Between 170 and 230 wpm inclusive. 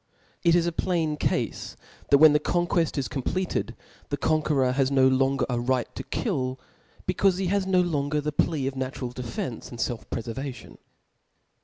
Yes: average, 175 wpm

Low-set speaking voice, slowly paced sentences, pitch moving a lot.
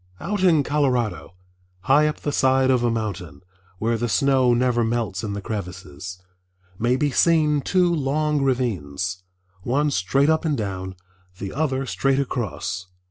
No: low, 125 Hz; average, 150 wpm; wide, 6.5 semitones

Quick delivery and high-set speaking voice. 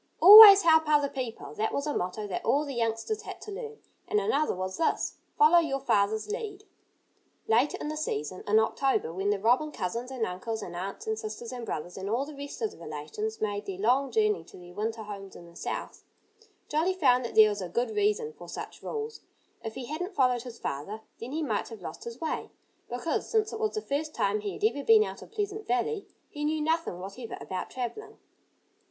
Yes: fast, 215 wpm; very high, 250 Hz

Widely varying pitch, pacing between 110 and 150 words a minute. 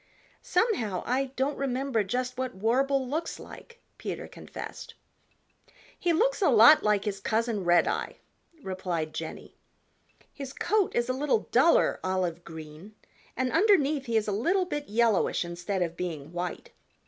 Yes: wide, 6.9 semitones; average, 145 wpm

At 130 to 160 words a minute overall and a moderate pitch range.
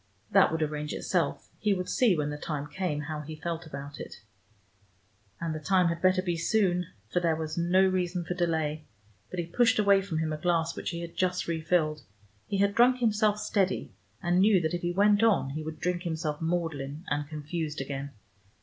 No: fast, 205 wpm; average, 3.1 semitones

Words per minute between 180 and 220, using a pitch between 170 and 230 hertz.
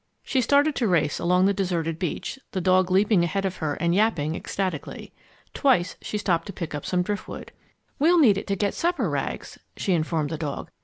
Yes: average, 200 wpm; medium, 185 Hz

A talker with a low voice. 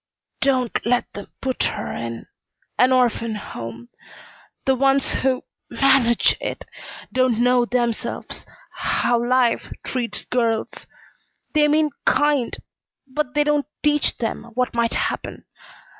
No: very high, 250 Hz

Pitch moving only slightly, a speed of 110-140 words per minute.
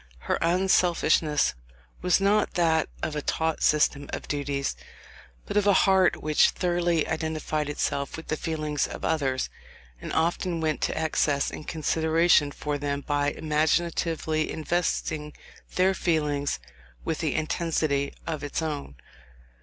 Yes: narrow, 2.2 semitones; slow, 135 wpm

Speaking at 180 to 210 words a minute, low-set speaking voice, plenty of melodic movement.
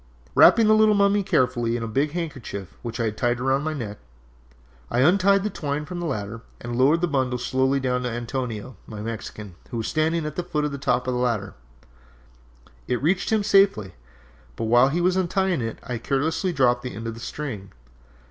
Yes: average, 200 wpm; low, 130 Hz; wide, 6.1 semitones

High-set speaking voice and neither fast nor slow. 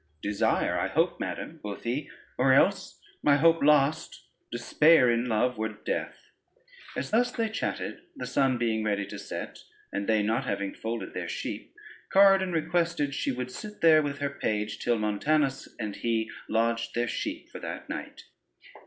No: low, 125 Hz; average, 165 wpm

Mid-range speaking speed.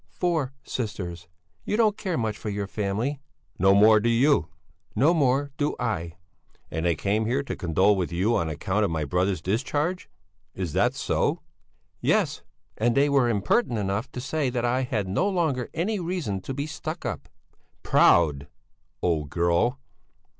Yes: average, 165 wpm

